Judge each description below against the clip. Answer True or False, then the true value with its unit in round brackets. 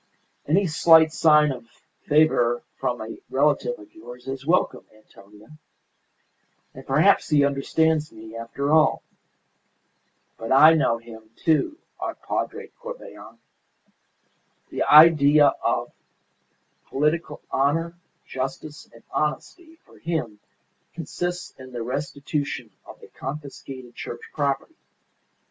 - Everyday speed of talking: False (110 wpm)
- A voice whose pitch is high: False (140 Hz)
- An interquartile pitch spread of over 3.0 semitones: True (4.3 semitones)